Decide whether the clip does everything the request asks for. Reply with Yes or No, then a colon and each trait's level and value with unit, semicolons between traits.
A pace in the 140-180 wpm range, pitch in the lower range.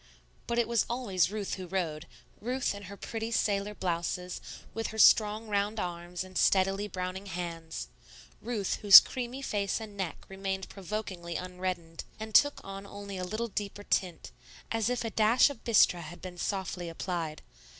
No: average, 165 wpm; high, 195 Hz